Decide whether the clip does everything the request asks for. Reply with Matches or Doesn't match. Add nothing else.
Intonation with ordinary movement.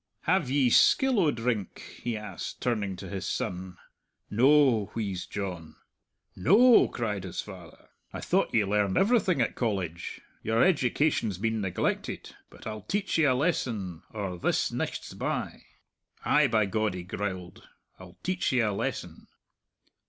Doesn't match